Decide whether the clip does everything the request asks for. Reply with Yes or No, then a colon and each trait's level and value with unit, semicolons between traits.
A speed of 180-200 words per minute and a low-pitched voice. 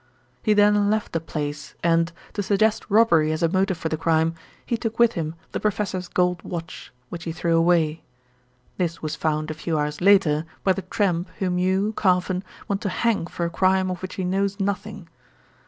No: average, 195 wpm; medium, 180 Hz